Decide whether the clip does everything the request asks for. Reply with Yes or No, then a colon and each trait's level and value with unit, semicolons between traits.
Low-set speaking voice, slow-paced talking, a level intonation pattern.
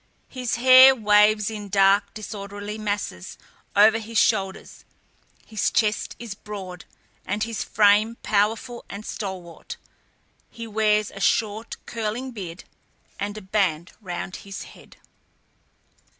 No: high, 210 Hz; slow, 120 wpm; narrow, 1.9 semitones